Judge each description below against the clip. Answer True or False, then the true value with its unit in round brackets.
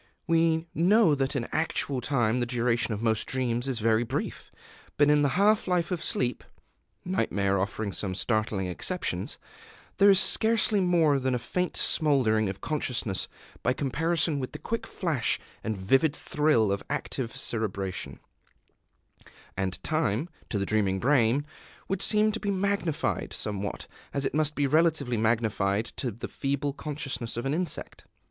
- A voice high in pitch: False (135 Hz)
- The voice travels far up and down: True (6.5 semitones)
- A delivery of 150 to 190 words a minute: True (155 wpm)